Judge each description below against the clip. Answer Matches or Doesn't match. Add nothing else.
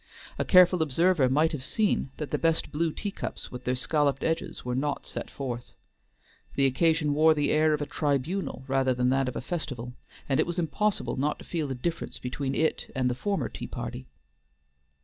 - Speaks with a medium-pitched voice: Matches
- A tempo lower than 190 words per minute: Doesn't match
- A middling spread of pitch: Matches